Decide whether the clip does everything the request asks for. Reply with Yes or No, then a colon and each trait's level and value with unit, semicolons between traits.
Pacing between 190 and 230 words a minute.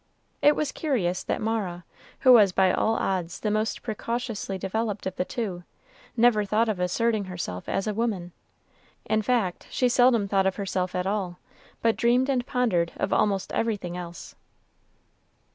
No: average, 160 wpm